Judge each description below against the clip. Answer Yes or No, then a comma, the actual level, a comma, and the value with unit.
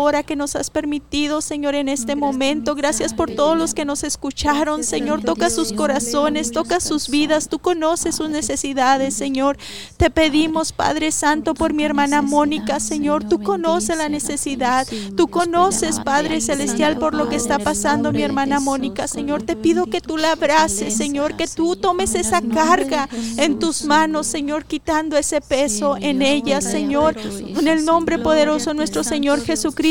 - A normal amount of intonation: No, narrow, 1.9 semitones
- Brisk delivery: No, average, 165 wpm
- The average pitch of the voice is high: Yes, very high, 300 Hz